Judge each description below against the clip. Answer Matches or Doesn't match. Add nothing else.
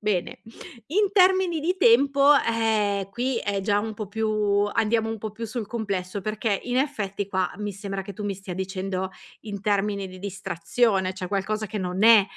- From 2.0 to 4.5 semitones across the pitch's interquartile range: Matches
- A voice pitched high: Matches